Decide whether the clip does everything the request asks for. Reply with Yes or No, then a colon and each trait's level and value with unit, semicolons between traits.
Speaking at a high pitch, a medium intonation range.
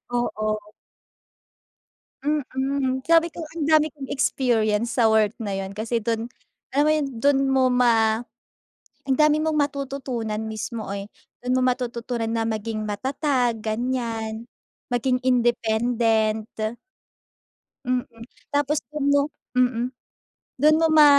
Yes: high, 245 Hz; average, 3.9 semitones